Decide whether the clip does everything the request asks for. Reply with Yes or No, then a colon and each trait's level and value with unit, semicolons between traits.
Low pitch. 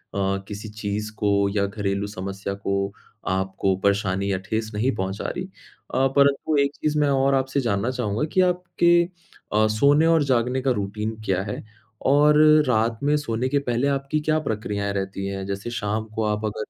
Yes: low, 110 Hz